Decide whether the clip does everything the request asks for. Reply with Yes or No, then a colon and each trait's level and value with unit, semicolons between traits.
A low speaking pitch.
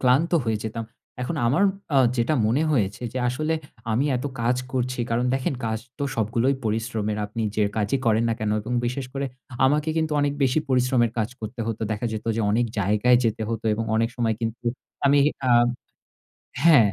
Yes: low, 120 Hz